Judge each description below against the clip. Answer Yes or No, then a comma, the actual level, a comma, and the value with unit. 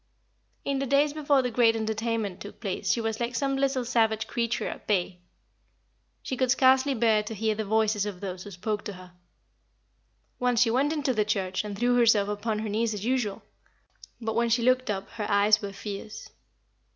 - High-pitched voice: Yes, high, 220 Hz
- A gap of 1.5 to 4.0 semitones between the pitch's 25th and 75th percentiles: Yes, average, 3.1 semitones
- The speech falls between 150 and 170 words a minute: No, average, 195 wpm